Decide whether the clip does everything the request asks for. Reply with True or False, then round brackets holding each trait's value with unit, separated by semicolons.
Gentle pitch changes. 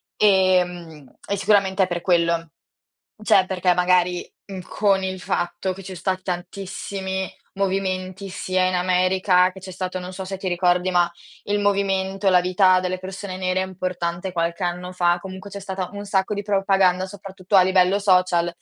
True (1.2 semitones)